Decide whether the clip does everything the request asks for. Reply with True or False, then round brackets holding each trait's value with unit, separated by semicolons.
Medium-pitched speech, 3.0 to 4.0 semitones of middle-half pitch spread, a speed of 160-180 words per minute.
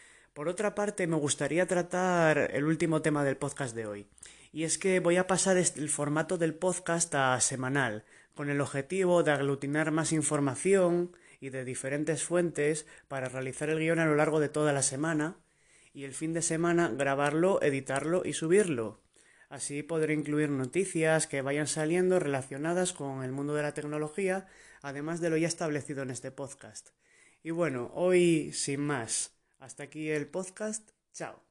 True (150 Hz; 3.5 semitones; 170 wpm)